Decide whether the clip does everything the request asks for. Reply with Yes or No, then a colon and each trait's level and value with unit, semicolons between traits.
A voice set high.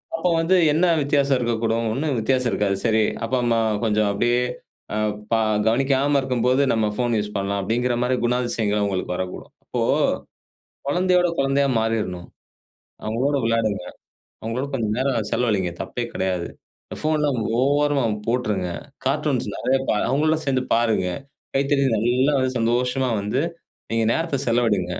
No: low, 120 Hz